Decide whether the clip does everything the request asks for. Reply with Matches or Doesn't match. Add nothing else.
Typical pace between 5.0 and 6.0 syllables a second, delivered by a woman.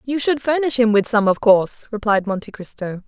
Matches